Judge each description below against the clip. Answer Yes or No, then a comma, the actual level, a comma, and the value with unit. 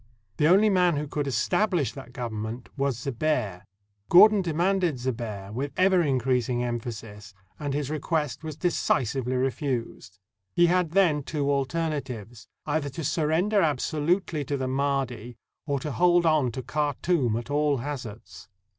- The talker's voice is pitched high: No, medium, 140 Hz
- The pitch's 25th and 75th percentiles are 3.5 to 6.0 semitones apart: Yes, average, 4.7 semitones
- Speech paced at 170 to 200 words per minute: No, average, 150 wpm